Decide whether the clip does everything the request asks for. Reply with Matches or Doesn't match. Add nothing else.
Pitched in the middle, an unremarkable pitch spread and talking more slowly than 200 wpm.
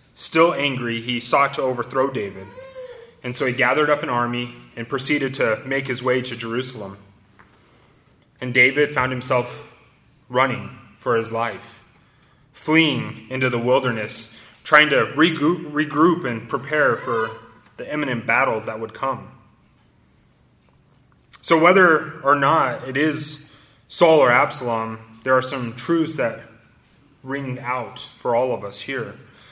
Doesn't match